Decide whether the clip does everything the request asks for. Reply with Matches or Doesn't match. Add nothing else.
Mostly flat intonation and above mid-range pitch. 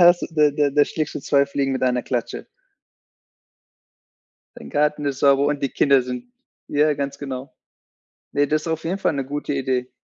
Doesn't match